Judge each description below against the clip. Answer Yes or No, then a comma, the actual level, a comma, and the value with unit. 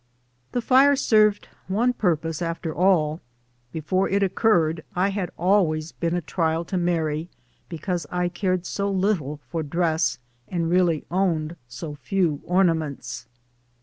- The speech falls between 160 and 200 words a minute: No, average, 140 wpm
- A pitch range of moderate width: Yes, average, 3.3 semitones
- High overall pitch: No, medium, 175 Hz